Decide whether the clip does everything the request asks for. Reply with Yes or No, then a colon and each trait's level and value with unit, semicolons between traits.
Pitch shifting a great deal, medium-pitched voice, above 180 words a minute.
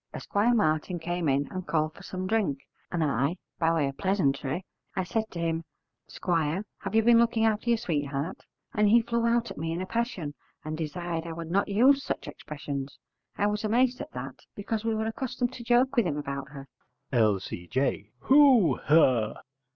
Yes: wide, 7.2 semitones; medium, 175 Hz; average, 190 wpm